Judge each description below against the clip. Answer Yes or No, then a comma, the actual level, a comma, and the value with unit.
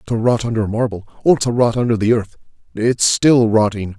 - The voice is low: Yes, low, 115 Hz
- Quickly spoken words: No, average, 180 wpm